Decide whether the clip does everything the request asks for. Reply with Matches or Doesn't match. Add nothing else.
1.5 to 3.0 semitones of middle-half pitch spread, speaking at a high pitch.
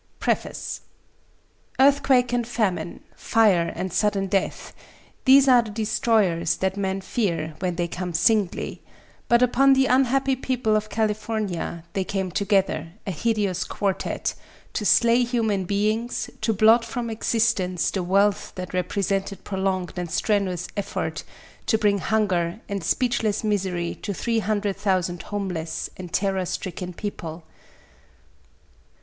Doesn't match